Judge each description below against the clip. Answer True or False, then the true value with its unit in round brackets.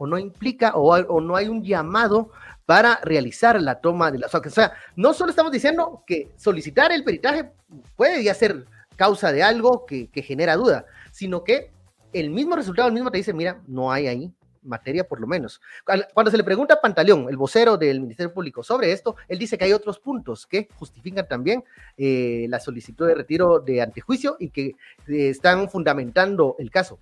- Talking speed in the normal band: False (195 wpm)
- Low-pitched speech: False (185 Hz)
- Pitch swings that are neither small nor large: False (7.4 semitones)